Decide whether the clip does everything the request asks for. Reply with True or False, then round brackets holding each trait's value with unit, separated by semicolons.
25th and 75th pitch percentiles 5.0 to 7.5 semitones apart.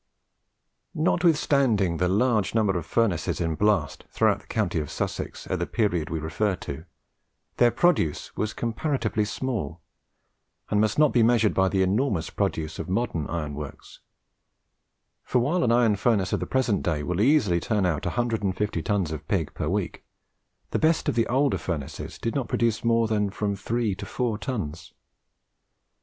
True (5.5 semitones)